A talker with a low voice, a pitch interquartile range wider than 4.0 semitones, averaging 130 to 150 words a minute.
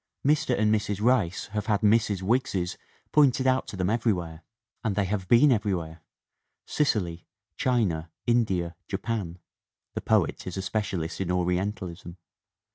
Yes: low, 100 Hz; average, 4.5 semitones; average, 140 wpm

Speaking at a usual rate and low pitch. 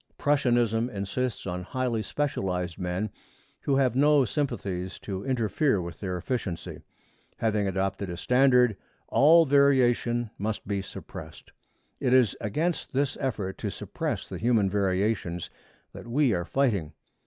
No: slow, 130 wpm; low, 115 Hz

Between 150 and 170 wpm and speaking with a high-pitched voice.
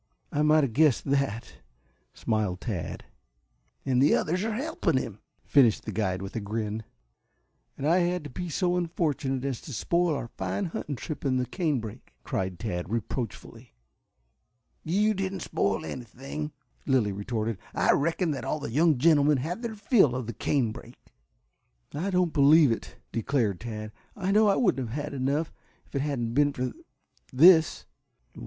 No: average, 160 wpm; medium, 140 Hz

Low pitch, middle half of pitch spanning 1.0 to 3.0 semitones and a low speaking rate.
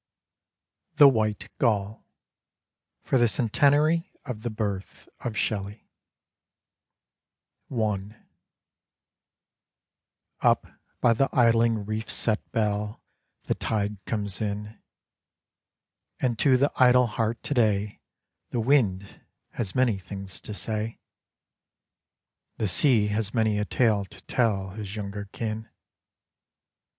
Yes: low, 110 Hz; narrow, 2.5 semitones; slow, 105 wpm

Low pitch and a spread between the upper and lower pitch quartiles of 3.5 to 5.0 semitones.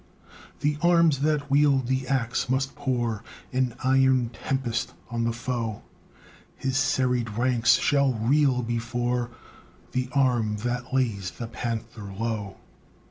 No: low, 125 Hz; narrow, 2.4 semitones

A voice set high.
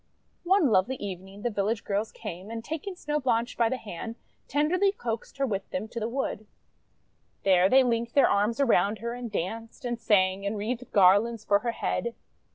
Yes: high, 230 Hz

